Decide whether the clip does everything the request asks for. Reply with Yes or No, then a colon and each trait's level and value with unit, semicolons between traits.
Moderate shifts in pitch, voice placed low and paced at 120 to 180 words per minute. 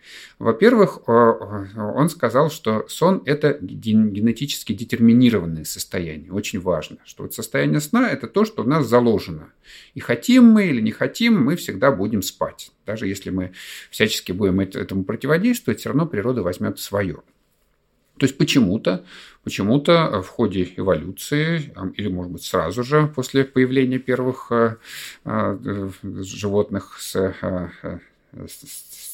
No: wide, 7.0 semitones; low, 115 Hz; average, 130 wpm